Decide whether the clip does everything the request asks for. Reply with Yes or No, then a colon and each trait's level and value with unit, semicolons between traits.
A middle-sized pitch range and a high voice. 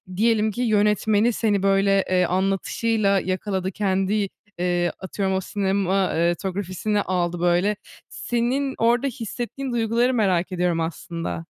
Yes: average, 3.1 semitones; high, 195 Hz